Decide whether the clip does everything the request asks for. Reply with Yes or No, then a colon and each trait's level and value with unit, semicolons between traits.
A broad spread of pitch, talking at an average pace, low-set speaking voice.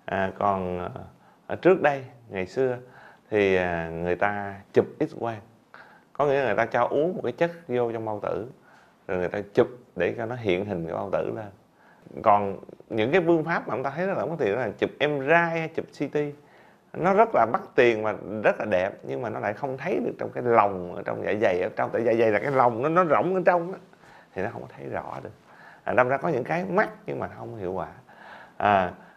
Yes: wide, 7.4 semitones; average, 235 wpm; low, 120 Hz